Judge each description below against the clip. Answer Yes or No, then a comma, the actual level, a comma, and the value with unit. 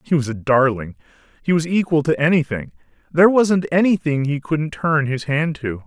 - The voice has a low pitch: No, medium, 150 Hz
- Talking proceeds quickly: No, average, 185 wpm